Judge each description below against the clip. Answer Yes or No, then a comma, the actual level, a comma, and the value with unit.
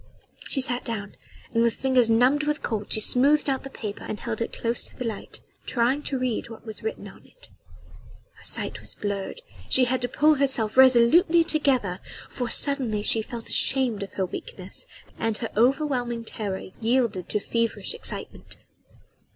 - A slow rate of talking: No, average, 175 wpm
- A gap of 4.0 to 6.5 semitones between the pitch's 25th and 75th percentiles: No, average, 3.5 semitones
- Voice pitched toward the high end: Yes, high, 245 Hz